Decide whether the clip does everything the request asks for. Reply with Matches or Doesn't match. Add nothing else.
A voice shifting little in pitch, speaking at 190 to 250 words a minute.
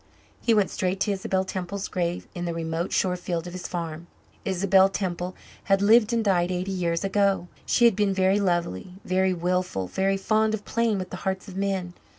Matches